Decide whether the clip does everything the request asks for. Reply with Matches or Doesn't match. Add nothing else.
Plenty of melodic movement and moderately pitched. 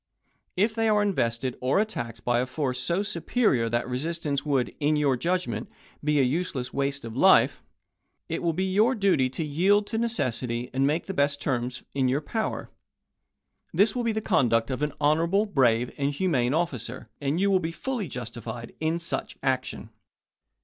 Matches